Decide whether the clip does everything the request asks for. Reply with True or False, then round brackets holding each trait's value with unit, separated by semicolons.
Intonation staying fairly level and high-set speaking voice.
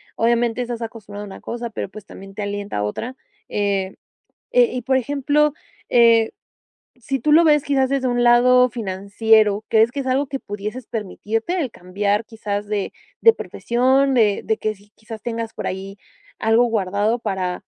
False (3.6 semitones; 225 Hz)